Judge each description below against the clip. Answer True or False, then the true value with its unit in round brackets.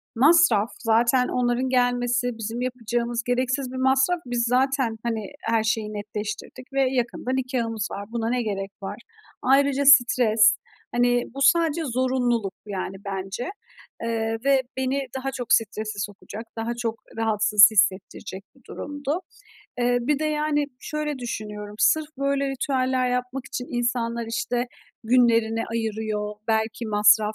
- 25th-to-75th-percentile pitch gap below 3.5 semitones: True (2.9 semitones)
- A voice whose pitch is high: True (240 Hz)